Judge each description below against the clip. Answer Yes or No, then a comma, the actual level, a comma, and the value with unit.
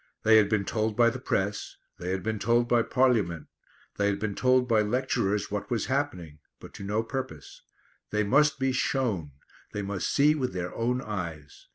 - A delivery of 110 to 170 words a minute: No, average, 190 wpm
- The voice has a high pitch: No, low, 110 Hz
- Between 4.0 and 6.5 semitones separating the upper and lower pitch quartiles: Yes, average, 4.3 semitones